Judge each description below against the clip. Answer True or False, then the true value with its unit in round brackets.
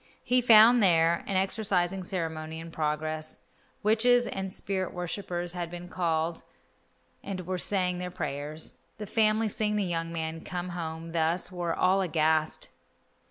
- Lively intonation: False (3.0 semitones)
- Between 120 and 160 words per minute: True (145 wpm)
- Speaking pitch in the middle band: True (175 Hz)